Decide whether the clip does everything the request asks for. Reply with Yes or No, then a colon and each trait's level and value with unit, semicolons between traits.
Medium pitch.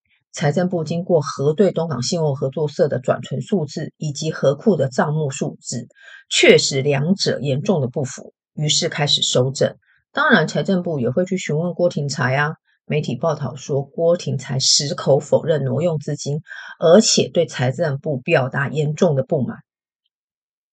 Yes: medium, 155 Hz